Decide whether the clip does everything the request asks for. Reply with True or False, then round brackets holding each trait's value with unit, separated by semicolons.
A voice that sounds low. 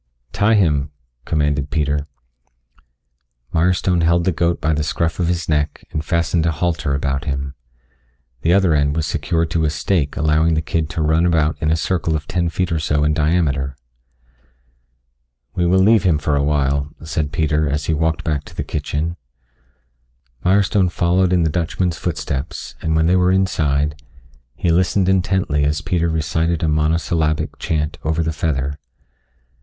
True (80 Hz)